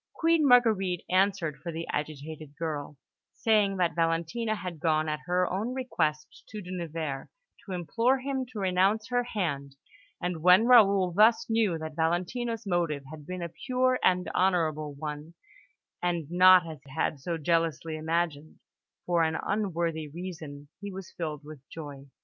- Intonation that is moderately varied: Yes, average, 4.2 semitones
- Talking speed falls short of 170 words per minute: Yes, average, 155 wpm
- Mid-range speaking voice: Yes, medium, 175 Hz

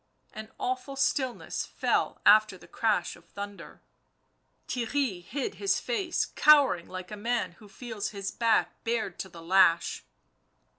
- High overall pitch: Yes, high, 215 Hz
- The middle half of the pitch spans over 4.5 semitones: Yes, average, 5.1 semitones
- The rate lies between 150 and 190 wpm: No, average, 140 wpm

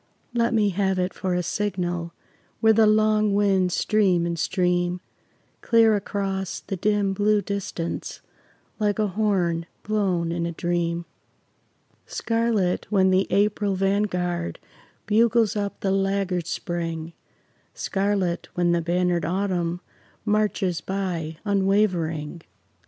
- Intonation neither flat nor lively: Yes, average, 3.0 semitones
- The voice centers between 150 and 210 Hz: Yes, high, 190 Hz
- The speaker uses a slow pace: Yes, slow, 120 wpm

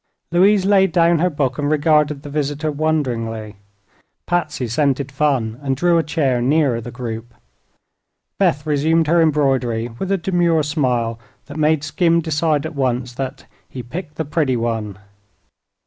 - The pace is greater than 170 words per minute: No, average, 150 wpm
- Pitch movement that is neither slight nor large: Yes, average, 4.3 semitones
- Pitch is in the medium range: Yes, medium, 145 Hz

